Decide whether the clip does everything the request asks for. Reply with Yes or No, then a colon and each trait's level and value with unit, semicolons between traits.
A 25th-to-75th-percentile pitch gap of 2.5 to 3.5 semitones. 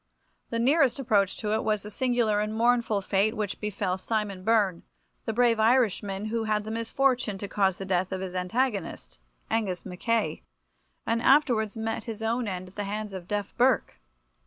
Yes: average, 2.9 semitones